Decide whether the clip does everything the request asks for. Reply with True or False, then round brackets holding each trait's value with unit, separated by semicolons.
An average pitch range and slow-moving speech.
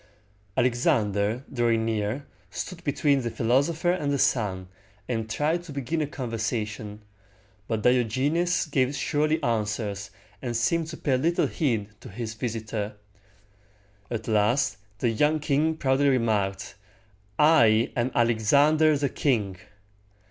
True (5.0 semitones; 125 wpm)